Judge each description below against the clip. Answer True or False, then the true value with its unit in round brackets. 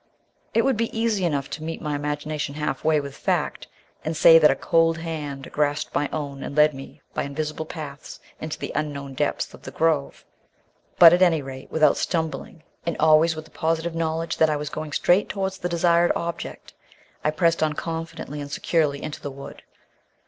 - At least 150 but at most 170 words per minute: False (190 wpm)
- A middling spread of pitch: False (2.2 semitones)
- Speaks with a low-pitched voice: False (155 Hz)